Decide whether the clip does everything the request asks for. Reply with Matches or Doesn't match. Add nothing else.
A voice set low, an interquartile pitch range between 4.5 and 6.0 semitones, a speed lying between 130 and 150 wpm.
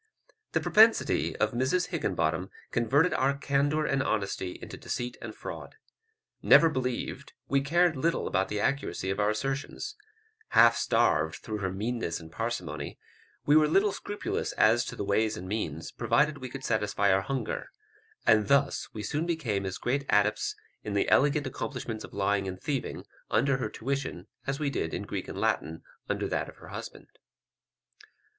Doesn't match